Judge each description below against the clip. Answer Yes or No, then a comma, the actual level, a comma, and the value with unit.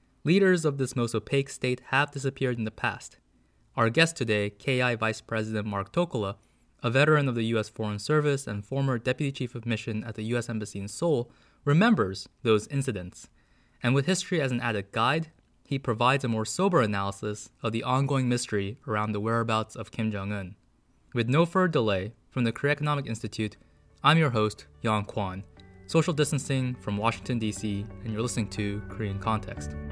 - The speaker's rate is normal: Yes, average, 180 wpm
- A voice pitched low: Yes, low, 115 Hz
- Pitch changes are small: No, average, 4.3 semitones